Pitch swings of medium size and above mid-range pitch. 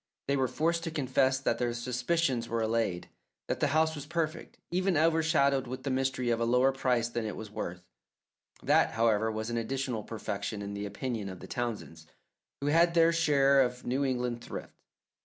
No: average, 3.7 semitones; low, 125 Hz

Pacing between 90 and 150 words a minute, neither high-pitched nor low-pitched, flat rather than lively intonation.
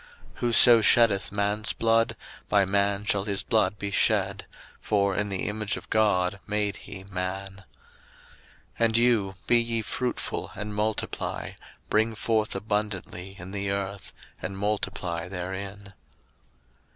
No: slow, 135 wpm; low, 100 Hz; narrow, 1.8 semitones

